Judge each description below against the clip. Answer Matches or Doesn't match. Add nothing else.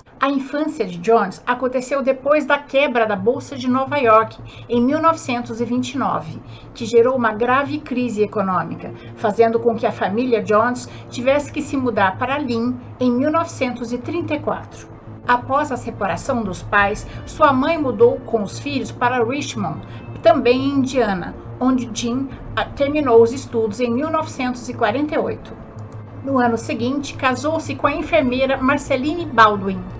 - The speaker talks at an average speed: Matches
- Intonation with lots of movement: Doesn't match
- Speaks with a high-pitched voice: Matches